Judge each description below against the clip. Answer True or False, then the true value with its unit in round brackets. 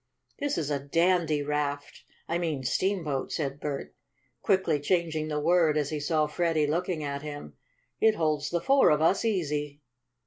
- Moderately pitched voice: True (155 Hz)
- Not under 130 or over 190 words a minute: True (165 wpm)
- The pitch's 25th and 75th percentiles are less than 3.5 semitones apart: True (2.9 semitones)